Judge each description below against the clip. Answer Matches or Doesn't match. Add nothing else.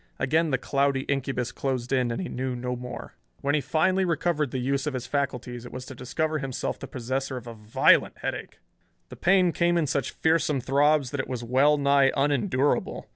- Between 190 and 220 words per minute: Matches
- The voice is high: Doesn't match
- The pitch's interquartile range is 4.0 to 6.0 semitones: Doesn't match